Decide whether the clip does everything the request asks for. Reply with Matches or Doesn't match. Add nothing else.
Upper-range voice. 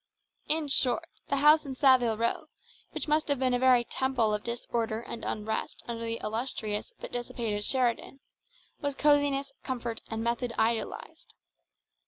Matches